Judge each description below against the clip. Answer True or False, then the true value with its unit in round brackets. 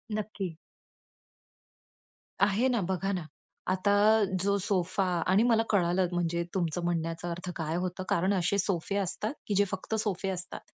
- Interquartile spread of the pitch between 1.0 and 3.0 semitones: True (2.6 semitones)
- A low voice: False (185 Hz)